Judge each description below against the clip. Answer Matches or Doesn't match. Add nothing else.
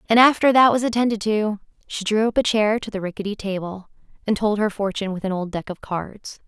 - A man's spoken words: Doesn't match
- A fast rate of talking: Matches